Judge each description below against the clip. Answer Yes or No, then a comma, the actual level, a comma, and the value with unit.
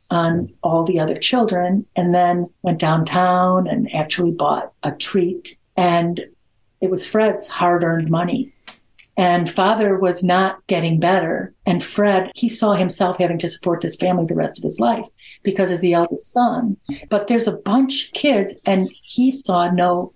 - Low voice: No, medium, 185 Hz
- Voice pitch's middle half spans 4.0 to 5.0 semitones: No, average, 2.9 semitones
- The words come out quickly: No, average, 165 wpm